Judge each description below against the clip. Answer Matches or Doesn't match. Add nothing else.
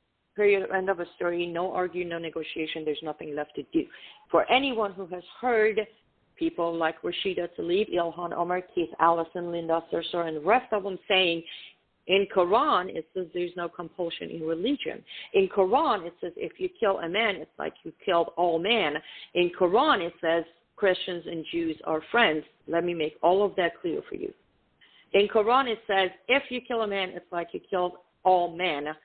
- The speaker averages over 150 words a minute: Matches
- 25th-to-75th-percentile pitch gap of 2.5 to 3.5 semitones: Doesn't match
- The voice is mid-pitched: Matches